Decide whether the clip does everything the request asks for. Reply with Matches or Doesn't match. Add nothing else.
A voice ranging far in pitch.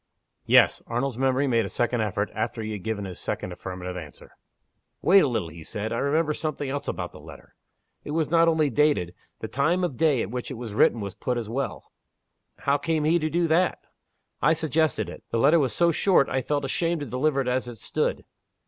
Matches